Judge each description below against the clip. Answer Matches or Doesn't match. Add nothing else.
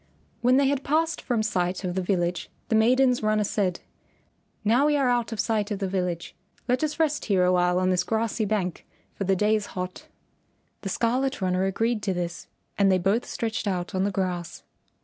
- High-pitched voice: Matches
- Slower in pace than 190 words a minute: Doesn't match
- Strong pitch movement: Doesn't match